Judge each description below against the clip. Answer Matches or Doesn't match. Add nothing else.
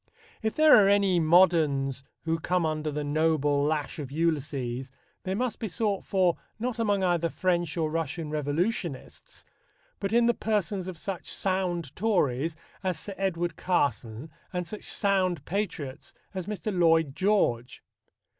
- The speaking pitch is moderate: Matches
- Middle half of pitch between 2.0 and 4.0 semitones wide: Doesn't match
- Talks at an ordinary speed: Matches